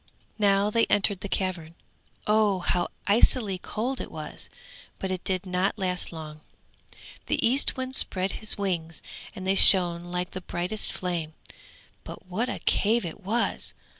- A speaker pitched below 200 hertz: Yes, high, 190 Hz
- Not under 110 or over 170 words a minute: Yes, average, 150 wpm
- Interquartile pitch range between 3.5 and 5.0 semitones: No, average, 2.9 semitones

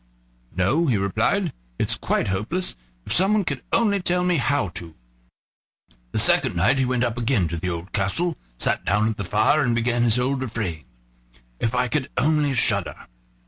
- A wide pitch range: Yes, wide, 6.6 semitones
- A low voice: Yes, low, 120 Hz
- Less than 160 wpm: No, average, 180 wpm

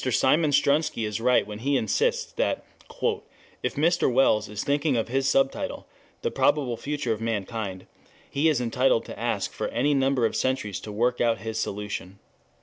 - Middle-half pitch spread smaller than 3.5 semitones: No, average, 4.1 semitones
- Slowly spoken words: No, average, 170 wpm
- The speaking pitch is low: Yes, low, 125 Hz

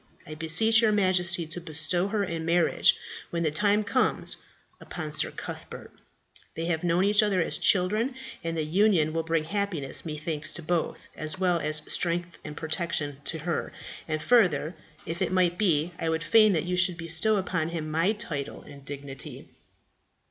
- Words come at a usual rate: Yes, average, 175 wpm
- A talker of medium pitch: Yes, medium, 170 Hz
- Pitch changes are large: No, average, 3.1 semitones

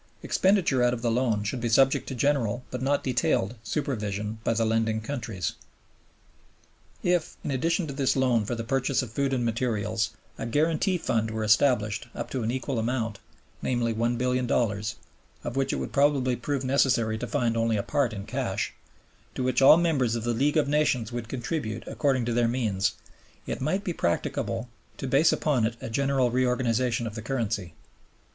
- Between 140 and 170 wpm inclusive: No, average, 180 wpm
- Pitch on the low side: Yes, low, 120 Hz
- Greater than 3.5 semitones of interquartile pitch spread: No, average, 3.1 semitones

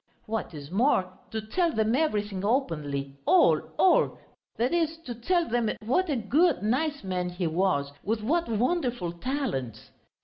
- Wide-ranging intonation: Yes, wide, 7.9 semitones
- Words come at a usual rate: Yes, average, 150 wpm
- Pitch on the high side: Yes, high, 225 Hz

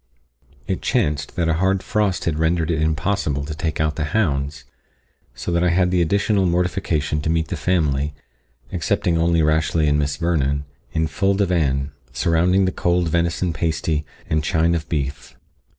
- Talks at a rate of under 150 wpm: No, average, 165 wpm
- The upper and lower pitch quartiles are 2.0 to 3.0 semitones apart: Yes, average, 2.7 semitones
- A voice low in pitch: Yes, very low, 80 Hz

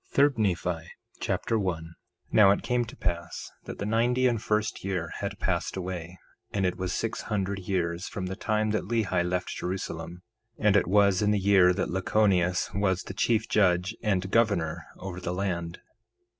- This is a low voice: Yes, very low, 95 Hz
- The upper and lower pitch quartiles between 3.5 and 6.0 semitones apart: No, average, 3.0 semitones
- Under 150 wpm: No, average, 185 wpm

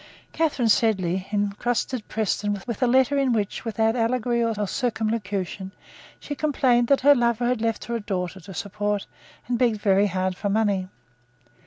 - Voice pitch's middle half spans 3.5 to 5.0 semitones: No, average, 3.1 semitones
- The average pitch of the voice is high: Yes, high, 220 Hz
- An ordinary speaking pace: Yes, average, 160 wpm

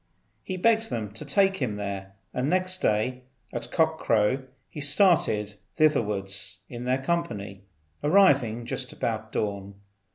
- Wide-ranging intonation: Yes, wide, 7.3 semitones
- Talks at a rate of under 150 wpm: Yes, slow, 135 wpm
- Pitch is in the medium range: No, low, 120 Hz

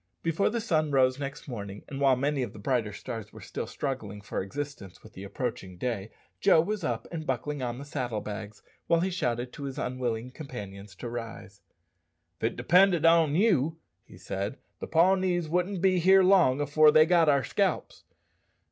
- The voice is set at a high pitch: No, low, 135 Hz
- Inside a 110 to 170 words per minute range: No, average, 185 wpm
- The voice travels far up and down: Yes, wide, 6.4 semitones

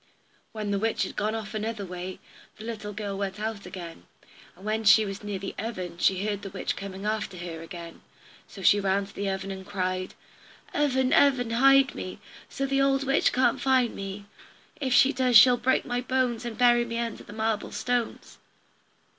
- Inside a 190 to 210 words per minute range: Yes, average, 195 wpm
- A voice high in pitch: Yes, high, 215 Hz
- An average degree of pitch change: Yes, average, 3.9 semitones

